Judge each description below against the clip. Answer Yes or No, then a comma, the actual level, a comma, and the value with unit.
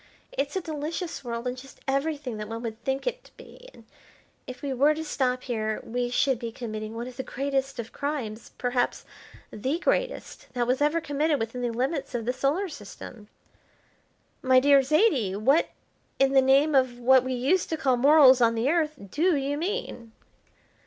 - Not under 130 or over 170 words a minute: No, average, 185 wpm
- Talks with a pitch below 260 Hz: No, very high, 265 Hz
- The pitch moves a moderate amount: Yes, average, 3.6 semitones